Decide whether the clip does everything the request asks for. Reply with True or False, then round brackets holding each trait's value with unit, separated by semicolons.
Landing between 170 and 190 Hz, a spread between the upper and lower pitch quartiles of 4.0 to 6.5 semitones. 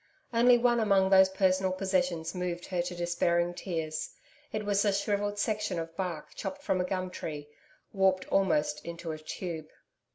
False (185 Hz; 2.7 semitones)